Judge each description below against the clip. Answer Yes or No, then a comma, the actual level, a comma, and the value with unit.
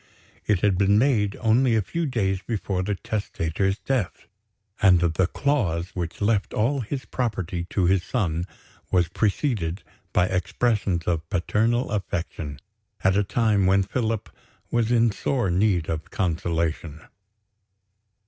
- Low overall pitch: Yes, low, 100 Hz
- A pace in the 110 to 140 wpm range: Yes, slow, 135 wpm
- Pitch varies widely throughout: No, average, 4.5 semitones